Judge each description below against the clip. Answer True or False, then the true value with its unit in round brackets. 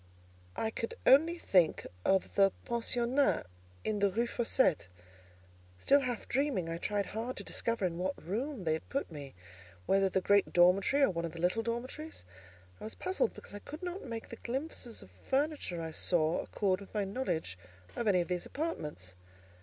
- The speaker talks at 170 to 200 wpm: True (180 wpm)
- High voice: True (205 Hz)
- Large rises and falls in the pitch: True (6.6 semitones)